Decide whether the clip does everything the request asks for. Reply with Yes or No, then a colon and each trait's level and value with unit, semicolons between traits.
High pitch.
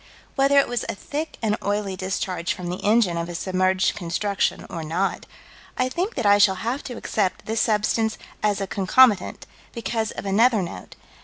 Yes: high, 205 Hz